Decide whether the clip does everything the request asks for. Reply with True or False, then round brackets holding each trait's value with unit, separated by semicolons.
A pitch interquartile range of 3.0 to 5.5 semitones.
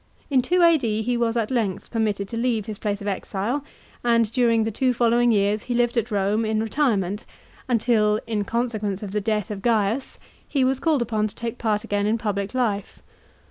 False (2.5 semitones)